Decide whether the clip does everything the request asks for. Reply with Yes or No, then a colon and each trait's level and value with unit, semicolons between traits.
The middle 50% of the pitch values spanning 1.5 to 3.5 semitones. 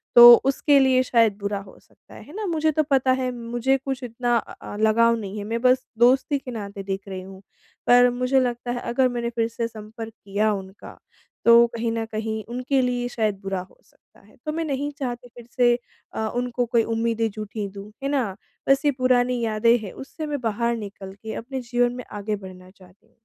Yes: average, 2.9 semitones